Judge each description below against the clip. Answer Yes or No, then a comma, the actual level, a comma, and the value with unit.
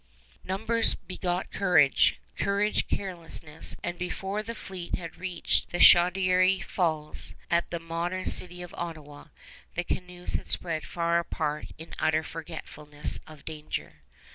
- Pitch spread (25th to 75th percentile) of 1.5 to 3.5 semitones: Yes, narrow, 2.5 semitones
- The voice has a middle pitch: Yes, medium, 175 Hz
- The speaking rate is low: Yes, slow, 130 wpm